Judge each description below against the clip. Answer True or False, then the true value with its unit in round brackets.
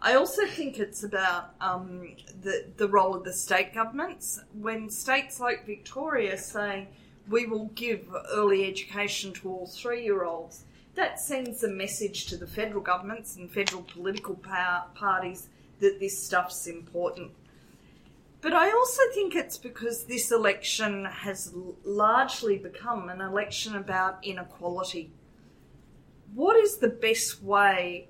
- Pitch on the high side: True (200 Hz)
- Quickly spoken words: False (140 wpm)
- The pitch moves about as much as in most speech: True (3.9 semitones)